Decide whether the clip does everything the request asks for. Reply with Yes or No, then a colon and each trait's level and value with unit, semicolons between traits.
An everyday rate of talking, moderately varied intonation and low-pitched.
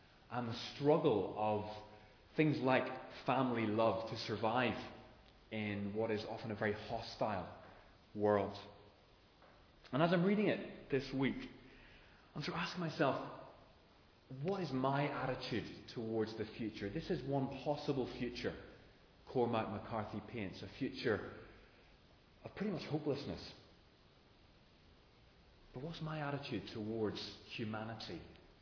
No: slow, 120 wpm; average, 4.1 semitones; low, 115 Hz